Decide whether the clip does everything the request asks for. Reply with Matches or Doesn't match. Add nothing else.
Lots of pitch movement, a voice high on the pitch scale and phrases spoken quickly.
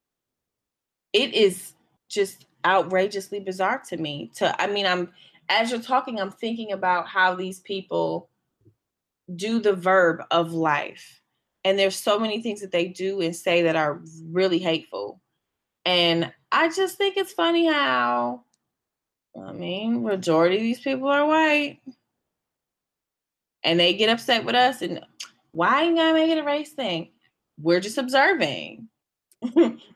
Doesn't match